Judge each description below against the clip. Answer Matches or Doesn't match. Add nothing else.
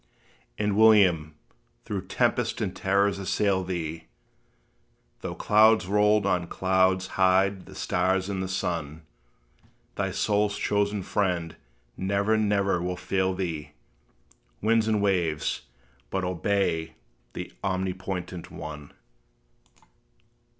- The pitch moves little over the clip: Matches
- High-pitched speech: Doesn't match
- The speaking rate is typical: Doesn't match